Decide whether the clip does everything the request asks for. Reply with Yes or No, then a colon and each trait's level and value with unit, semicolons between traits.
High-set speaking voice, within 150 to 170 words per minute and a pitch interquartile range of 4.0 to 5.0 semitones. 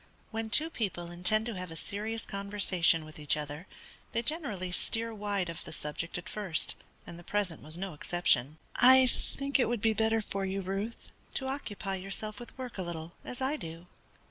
No: high, 200 Hz; average, 195 wpm; average, 4.6 semitones